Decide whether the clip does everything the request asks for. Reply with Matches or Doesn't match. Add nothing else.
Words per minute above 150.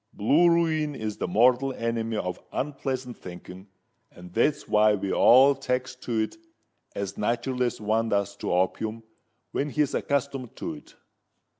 Doesn't match